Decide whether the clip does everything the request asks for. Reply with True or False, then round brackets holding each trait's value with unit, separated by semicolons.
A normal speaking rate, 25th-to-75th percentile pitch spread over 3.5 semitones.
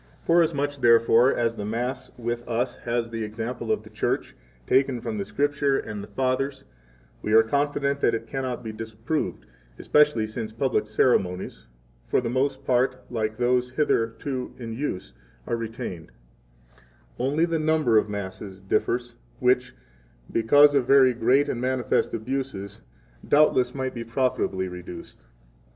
False (150 wpm; 3.2 semitones)